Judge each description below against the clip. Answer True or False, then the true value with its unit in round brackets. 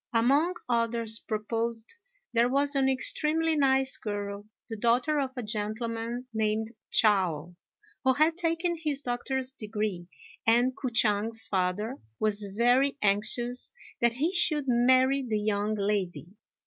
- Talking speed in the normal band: False (130 wpm)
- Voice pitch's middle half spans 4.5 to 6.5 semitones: False (3.9 semitones)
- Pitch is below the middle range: False (235 Hz)